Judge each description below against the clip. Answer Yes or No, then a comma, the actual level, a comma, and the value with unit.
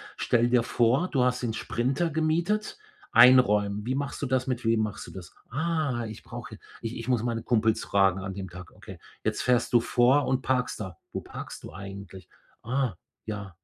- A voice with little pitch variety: No, average, 4.0 semitones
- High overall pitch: No, low, 120 Hz